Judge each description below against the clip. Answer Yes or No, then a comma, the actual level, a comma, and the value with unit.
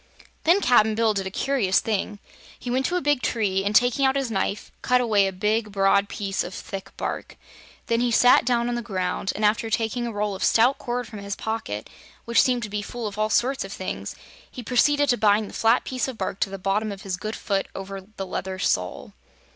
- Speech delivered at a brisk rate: Yes, fast, 230 wpm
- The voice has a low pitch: No, high, 215 Hz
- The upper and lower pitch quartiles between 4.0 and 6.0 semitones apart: No, average, 3.6 semitones